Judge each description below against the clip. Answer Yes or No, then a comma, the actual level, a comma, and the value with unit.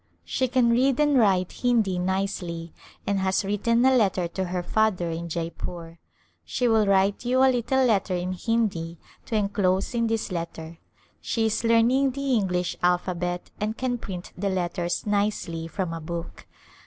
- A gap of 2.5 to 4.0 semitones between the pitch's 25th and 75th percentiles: No, average, 4.7 semitones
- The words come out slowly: No, average, 165 wpm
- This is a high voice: Yes, high, 195 Hz